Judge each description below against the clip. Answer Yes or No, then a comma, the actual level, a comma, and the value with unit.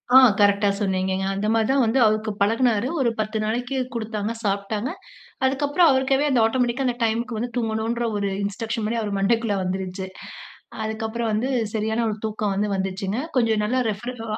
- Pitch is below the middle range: No, high, 220 Hz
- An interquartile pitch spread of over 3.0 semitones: No, narrow, 2.6 semitones